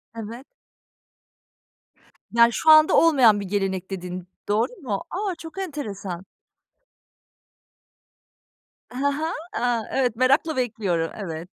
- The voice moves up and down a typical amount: No, wide, 6.9 semitones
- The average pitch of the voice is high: Yes, high, 235 Hz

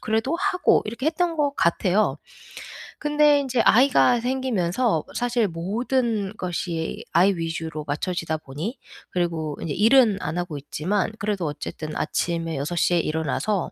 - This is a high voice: Yes, high, 195 Hz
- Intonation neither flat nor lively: No, wide, 7.0 semitones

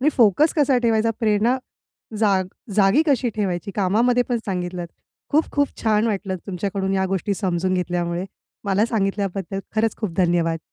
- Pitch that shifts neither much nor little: Yes, average, 3.5 semitones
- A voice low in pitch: No, high, 200 Hz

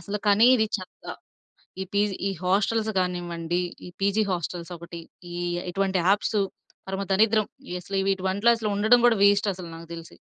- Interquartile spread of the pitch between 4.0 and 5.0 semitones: No, average, 2.7 semitones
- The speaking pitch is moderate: No, high, 195 Hz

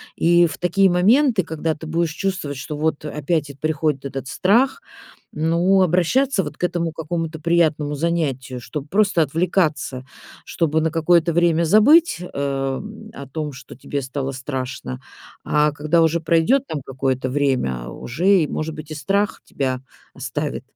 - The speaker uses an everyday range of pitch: Yes, average, 3.7 semitones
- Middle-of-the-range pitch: Yes, medium, 155 Hz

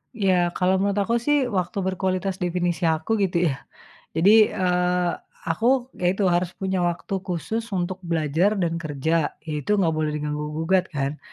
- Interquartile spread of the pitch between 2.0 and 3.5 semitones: Yes, narrow, 2.6 semitones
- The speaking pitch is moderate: Yes, medium, 180 Hz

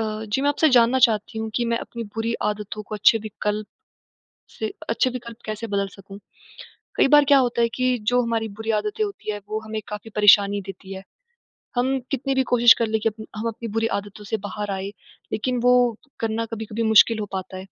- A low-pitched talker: No, high, 220 Hz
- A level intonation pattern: Yes, narrow, 2.1 semitones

